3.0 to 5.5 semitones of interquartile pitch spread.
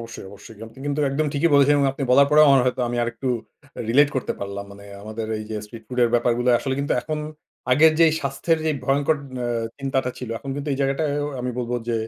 Yes: average, 3.3 semitones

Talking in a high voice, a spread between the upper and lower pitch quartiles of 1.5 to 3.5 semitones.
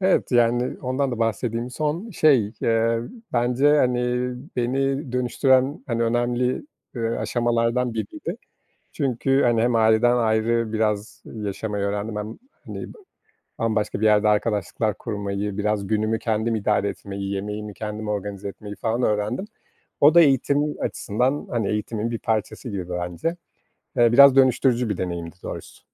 No: low, 115 Hz; average, 3.0 semitones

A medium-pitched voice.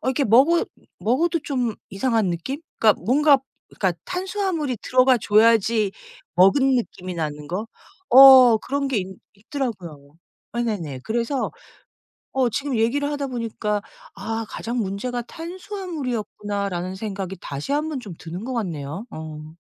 No: high, 230 Hz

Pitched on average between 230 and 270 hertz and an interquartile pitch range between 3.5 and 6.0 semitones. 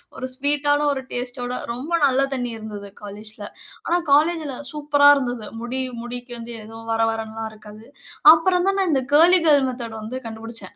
Yes: high, 245 Hz; average, 4.5 semitones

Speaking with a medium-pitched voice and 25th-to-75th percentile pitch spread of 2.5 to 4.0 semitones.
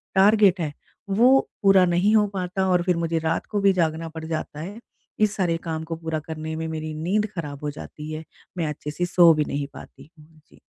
Yes: medium, 165 Hz; average, 3.3 semitones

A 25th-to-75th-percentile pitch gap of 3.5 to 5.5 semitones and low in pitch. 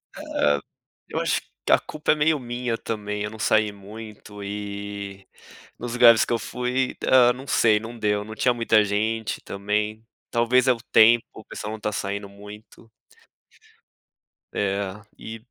No: narrow, 2.5 semitones; low, 110 Hz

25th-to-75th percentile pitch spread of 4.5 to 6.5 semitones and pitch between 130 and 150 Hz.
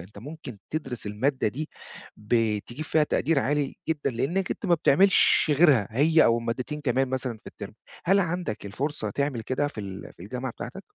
Yes: average, 5.2 semitones; low, 135 Hz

